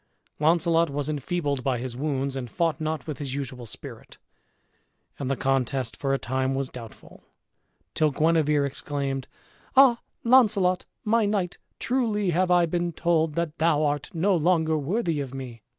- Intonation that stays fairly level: No, average, 4.3 semitones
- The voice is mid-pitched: Yes, medium, 155 Hz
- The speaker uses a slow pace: No, average, 155 wpm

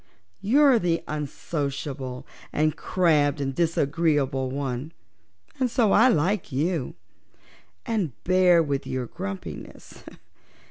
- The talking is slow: Yes, slow, 100 wpm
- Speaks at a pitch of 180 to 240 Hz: No, medium, 155 Hz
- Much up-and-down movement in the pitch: No, average, 5.0 semitones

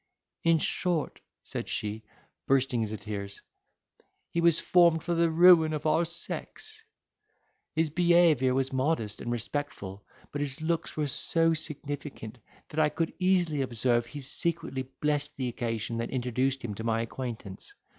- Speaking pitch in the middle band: Yes, medium, 145 Hz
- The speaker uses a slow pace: No, average, 145 wpm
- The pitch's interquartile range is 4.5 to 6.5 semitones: Yes, wide, 5.5 semitones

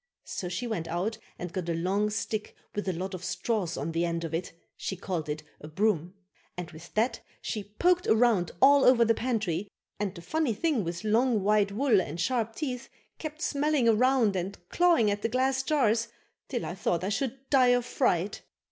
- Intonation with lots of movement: Yes, wide, 5.8 semitones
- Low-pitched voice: No, high, 210 Hz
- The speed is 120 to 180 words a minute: No, average, 200 wpm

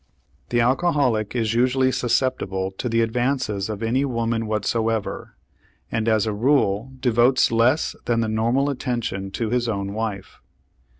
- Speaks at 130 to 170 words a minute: Yes, average, 140 wpm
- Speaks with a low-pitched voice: Yes, low, 115 Hz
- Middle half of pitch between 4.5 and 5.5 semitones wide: No, average, 2.7 semitones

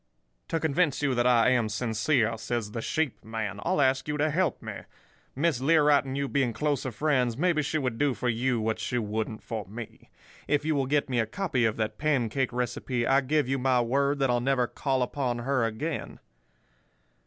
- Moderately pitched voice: No, low, 130 Hz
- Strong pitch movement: No, average, 3.7 semitones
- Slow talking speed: No, average, 200 wpm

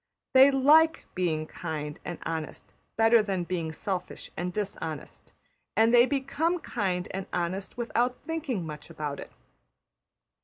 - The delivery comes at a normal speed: No, slow, 130 wpm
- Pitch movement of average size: No, wide, 7.2 semitones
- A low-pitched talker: No, high, 190 Hz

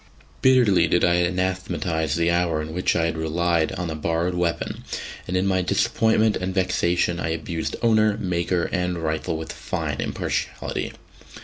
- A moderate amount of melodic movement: No, narrow, 2.0 semitones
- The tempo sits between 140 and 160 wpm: Yes, average, 155 wpm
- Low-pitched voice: Yes, very low, 85 Hz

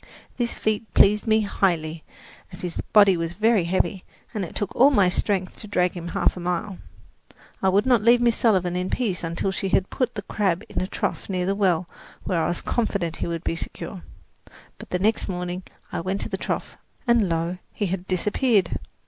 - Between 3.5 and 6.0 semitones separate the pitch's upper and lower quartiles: No, average, 3.1 semitones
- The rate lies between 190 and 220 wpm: Yes, average, 200 wpm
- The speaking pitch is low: No, high, 190 Hz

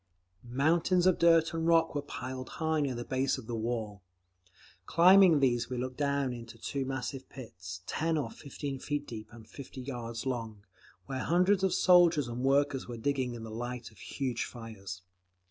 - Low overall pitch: Yes, low, 130 Hz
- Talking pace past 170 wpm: Yes, average, 180 wpm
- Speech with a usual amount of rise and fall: Yes, average, 4.4 semitones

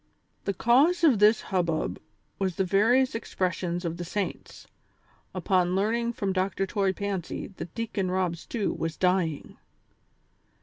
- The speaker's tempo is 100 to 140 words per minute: Yes, slow, 135 wpm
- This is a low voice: No, high, 190 Hz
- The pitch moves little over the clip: No, average, 3.3 semitones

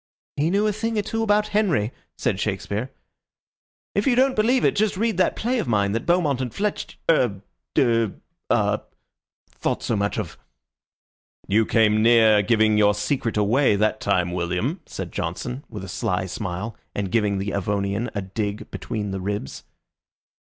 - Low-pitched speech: Yes, low, 110 Hz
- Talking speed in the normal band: Yes, average, 165 wpm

